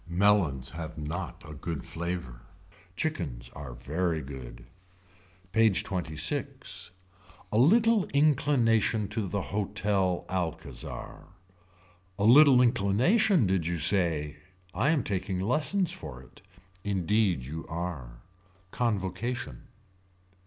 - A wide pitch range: Yes, wide, 6.5 semitones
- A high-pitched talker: No, very low, 95 Hz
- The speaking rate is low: Yes, slow, 105 wpm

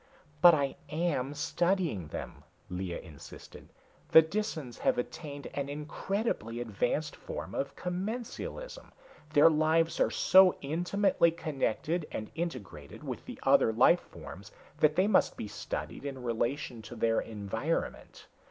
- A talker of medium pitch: Yes, medium, 145 Hz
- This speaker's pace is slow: Yes, slow, 130 wpm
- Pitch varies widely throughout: Yes, wide, 7.0 semitones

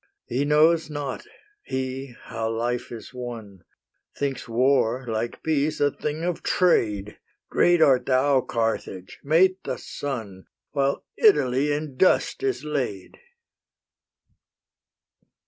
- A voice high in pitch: No, low, 135 Hz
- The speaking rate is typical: No, slow, 110 wpm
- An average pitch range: Yes, average, 4.3 semitones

